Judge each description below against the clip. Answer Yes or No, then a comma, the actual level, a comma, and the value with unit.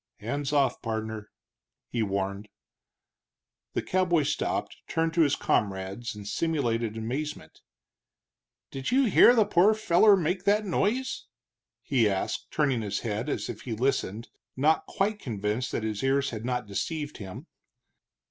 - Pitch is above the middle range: No, low, 130 Hz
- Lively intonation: Yes, wide, 7.2 semitones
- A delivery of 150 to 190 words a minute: No, average, 140 wpm